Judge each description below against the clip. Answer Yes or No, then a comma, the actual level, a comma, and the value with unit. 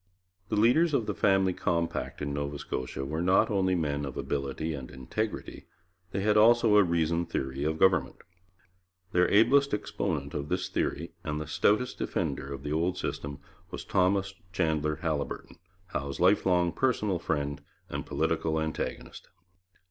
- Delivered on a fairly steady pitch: No, average, 5.2 semitones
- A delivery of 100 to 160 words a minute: Yes, average, 150 wpm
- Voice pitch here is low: Yes, very low, 85 Hz